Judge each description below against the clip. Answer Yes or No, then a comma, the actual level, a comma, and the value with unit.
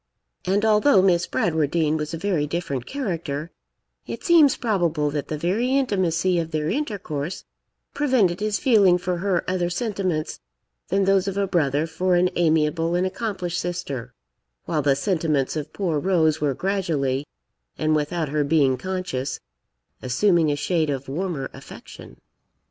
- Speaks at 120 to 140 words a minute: No, average, 150 wpm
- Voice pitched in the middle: Yes, medium, 170 Hz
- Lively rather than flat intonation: No, average, 4.1 semitones